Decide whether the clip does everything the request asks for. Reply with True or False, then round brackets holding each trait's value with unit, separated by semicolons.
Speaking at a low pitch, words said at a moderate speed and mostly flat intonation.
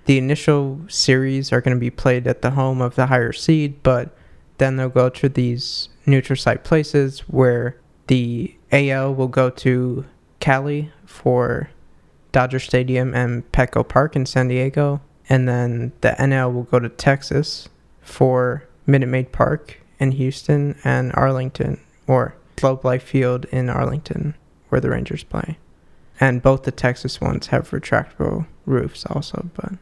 True (130 Hz; 155 wpm; 1.8 semitones)